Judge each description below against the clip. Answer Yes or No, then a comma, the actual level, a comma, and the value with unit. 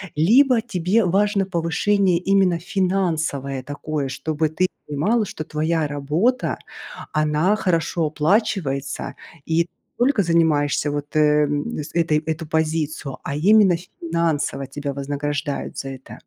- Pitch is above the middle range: No, medium, 160 Hz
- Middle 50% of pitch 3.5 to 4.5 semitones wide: Yes, average, 4.1 semitones